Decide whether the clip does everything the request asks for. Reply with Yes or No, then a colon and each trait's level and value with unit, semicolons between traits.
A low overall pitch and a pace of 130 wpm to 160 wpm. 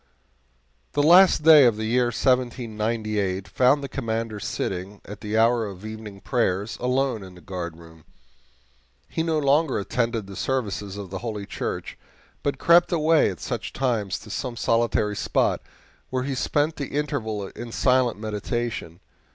Yes: low, 115 Hz; average, 150 wpm